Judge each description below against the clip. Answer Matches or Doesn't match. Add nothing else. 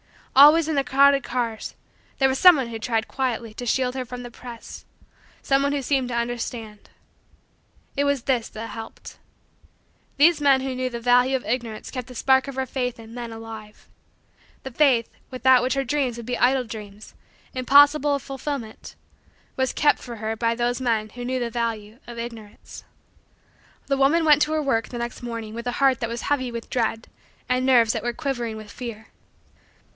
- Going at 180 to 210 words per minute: Matches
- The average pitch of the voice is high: Matches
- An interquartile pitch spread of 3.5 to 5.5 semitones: Doesn't match